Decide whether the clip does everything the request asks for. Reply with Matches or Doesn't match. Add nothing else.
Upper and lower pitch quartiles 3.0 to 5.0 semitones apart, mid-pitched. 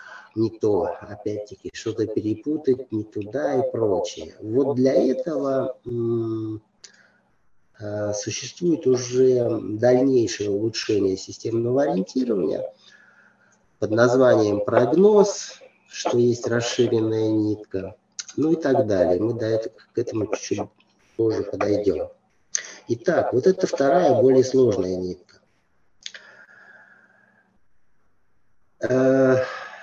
Doesn't match